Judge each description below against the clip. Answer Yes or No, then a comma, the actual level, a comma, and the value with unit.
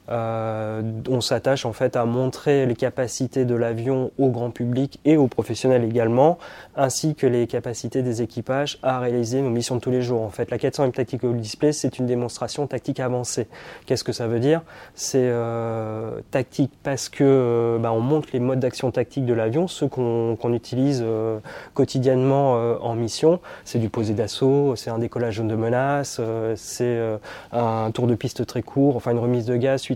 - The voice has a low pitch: Yes, low, 125 Hz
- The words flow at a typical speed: Yes, average, 190 wpm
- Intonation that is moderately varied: No, narrow, 2.3 semitones